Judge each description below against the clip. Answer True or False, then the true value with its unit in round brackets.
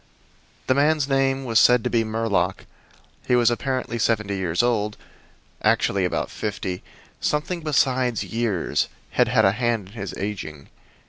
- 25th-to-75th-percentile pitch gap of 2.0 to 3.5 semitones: False (4.3 semitones)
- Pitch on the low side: True (115 Hz)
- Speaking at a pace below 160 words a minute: True (145 wpm)